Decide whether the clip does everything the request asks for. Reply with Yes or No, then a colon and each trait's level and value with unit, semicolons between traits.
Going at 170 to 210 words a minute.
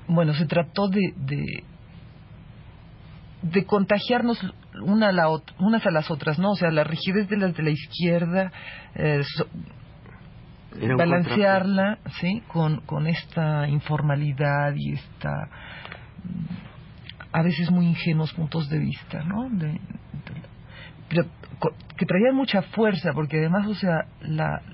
No: average, 135 wpm